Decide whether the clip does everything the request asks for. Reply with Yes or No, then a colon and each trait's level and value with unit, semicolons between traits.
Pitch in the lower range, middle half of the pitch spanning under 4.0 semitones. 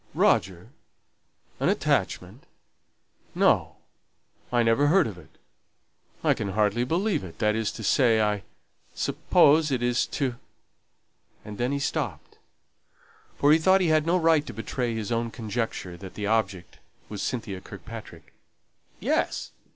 No: low, 115 Hz; wide, 5.4 semitones